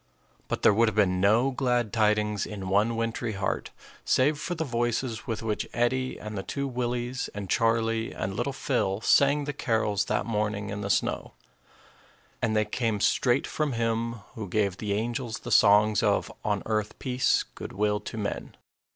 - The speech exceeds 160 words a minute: Yes, average, 175 wpm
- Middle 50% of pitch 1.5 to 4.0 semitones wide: Yes, average, 2.8 semitones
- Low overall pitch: Yes, low, 115 Hz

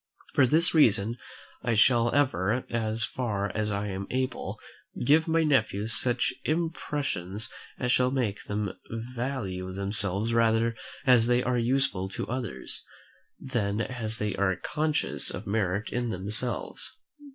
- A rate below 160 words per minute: Yes, slow, 135 wpm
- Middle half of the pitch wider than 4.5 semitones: No, average, 4.0 semitones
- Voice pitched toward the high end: No, low, 115 Hz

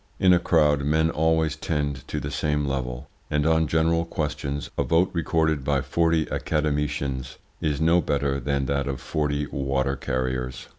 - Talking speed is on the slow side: No, average, 160 wpm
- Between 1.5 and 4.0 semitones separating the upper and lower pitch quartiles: Yes, narrow, 2.6 semitones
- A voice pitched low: Yes, very low, 75 Hz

